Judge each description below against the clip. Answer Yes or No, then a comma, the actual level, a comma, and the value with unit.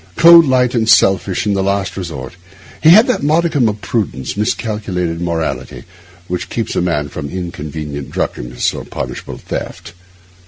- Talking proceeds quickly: No, average, 150 wpm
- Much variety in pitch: Yes, wide, 6.3 semitones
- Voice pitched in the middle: No, very low, 95 Hz